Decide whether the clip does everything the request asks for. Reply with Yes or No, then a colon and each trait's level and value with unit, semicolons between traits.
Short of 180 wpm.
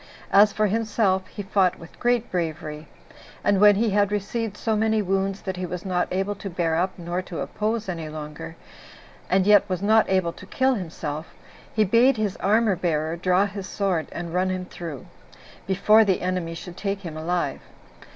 No: average, 185 wpm